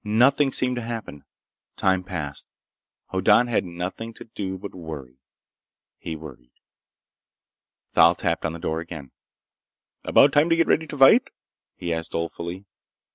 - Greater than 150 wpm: No, average, 140 wpm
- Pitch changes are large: Yes, wide, 6.3 semitones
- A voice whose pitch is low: Yes, very low, 95 Hz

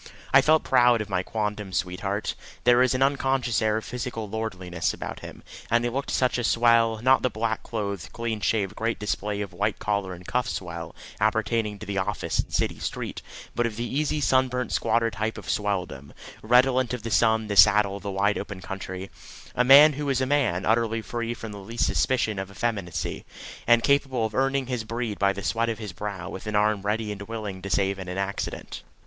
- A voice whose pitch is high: No, low, 110 Hz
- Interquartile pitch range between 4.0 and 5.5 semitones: No, average, 3.2 semitones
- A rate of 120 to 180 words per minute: No, fast, 205 wpm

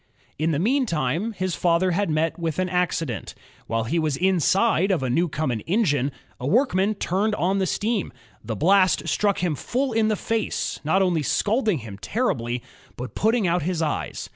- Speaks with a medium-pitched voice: Yes, medium, 180 Hz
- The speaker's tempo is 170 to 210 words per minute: Yes, average, 175 wpm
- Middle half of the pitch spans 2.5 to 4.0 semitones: No, average, 5.1 semitones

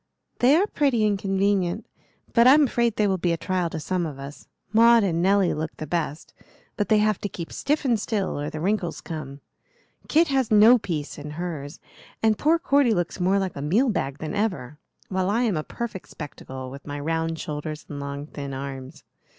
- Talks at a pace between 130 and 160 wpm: No, fast, 205 wpm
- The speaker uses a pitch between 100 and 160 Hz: No, medium, 185 Hz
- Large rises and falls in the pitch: Yes, wide, 6.4 semitones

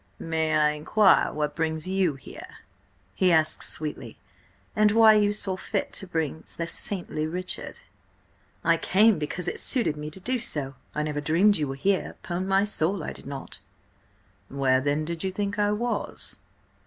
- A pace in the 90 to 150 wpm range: No, average, 170 wpm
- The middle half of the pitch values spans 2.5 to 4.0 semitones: No, average, 4.9 semitones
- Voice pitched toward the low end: No, medium, 170 Hz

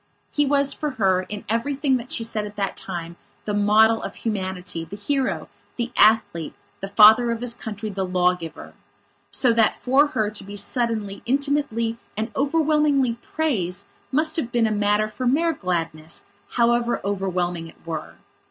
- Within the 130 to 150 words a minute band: No, average, 165 wpm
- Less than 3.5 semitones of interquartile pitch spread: No, average, 4.9 semitones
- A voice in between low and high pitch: No, high, 220 Hz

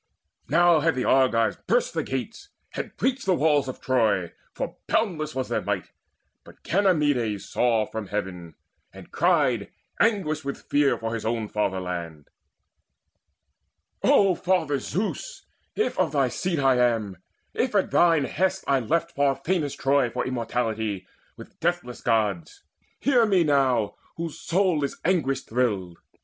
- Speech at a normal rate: Yes, average, 145 wpm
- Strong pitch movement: Yes, wide, 6.9 semitones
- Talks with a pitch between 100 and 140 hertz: Yes, low, 135 Hz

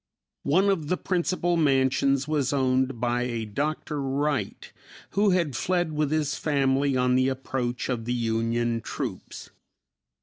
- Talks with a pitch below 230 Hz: Yes, low, 135 Hz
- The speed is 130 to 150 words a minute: Yes, average, 140 wpm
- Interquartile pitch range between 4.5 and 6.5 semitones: No, average, 3.7 semitones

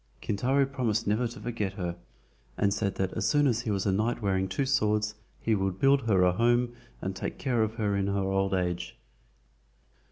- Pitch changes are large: No, average, 3.7 semitones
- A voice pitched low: Yes, low, 105 Hz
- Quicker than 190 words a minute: Yes, average, 200 wpm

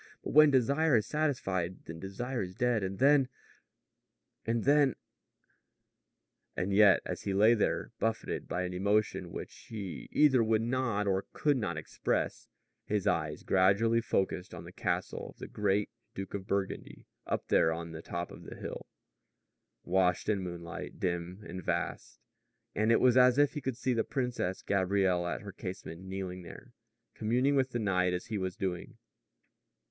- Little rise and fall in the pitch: No, average, 4.8 semitones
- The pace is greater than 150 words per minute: Yes, average, 165 wpm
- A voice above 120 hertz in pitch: No, low, 100 Hz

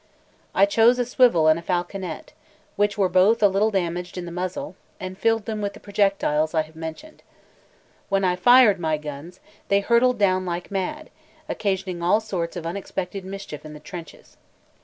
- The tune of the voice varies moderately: Yes, average, 3.1 semitones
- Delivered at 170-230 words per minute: Yes, average, 180 wpm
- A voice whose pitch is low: No, medium, 185 Hz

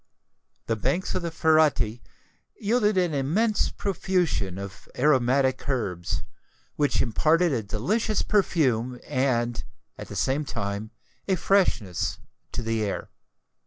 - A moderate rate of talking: No, slow, 120 wpm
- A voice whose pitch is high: No, low, 135 Hz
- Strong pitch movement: Yes, wide, 7.7 semitones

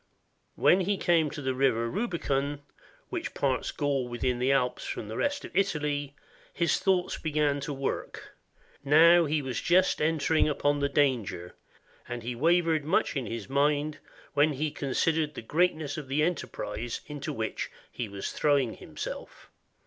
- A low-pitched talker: No, medium, 145 Hz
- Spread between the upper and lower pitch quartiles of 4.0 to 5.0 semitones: No, average, 3.4 semitones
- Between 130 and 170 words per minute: Yes, average, 155 wpm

